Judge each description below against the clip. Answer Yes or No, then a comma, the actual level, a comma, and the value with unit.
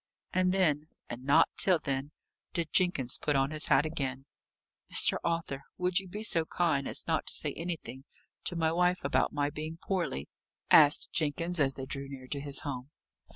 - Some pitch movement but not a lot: Yes, average, 3.9 semitones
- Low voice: No, medium, 150 Hz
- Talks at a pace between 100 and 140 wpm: No, average, 185 wpm